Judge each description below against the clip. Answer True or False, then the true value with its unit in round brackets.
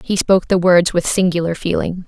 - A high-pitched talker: False (175 Hz)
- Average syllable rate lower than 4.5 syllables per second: False (5.6 syllables/s)